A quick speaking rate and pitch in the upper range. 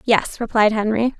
No: average, 150 wpm; high, 220 Hz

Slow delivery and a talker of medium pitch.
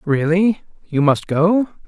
Yes: slow, 95 wpm; medium, 175 Hz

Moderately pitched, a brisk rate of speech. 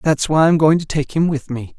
Yes: medium, 150 Hz; fast, 305 wpm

